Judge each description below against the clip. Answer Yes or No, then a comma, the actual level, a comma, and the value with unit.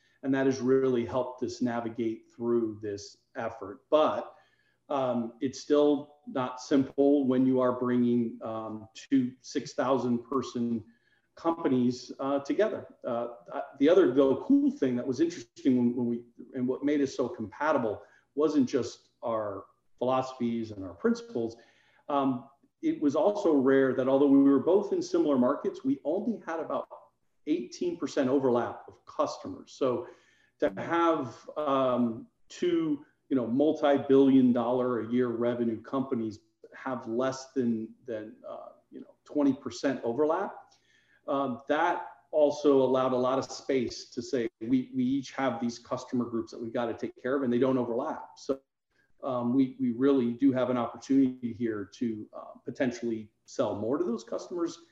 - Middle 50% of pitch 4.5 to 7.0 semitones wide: No, average, 3.4 semitones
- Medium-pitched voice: No, low, 130 Hz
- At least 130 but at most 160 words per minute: Yes, average, 155 wpm